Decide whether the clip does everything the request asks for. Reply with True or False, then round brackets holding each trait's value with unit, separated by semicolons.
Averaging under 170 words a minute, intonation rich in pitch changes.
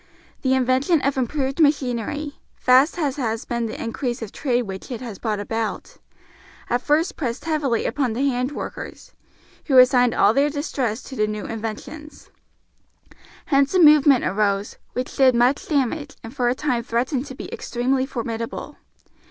False (160 wpm; 3.5 semitones)